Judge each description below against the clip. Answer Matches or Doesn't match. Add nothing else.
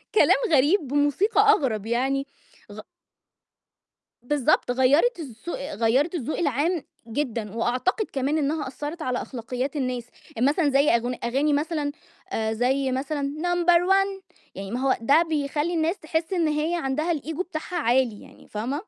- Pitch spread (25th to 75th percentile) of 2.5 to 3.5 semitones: Doesn't match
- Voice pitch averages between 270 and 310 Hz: Matches